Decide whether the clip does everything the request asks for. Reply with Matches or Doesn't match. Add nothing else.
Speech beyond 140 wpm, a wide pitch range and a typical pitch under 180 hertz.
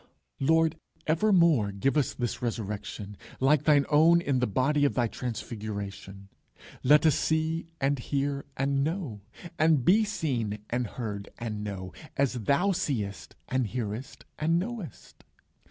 Doesn't match